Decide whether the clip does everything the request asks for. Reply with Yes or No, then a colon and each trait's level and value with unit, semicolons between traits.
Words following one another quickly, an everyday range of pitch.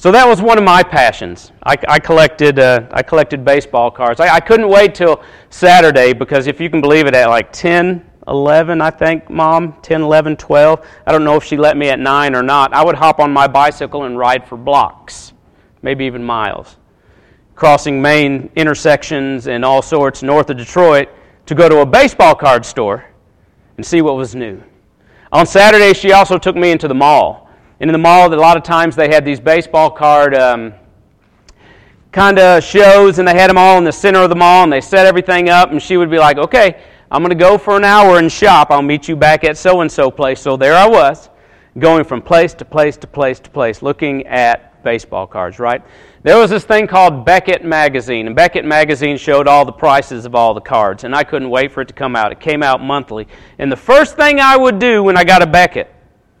Yes: fast, 220 wpm; average, 4.6 semitones